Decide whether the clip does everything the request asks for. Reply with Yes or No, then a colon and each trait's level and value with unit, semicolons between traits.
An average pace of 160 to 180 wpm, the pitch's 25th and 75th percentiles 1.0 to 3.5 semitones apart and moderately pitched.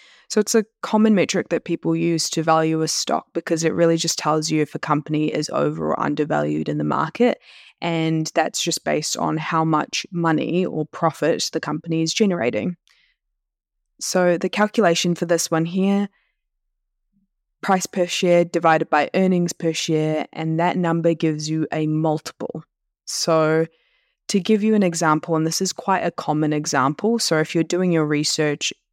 Yes: average, 170 wpm; narrow, 2.4 semitones; medium, 165 Hz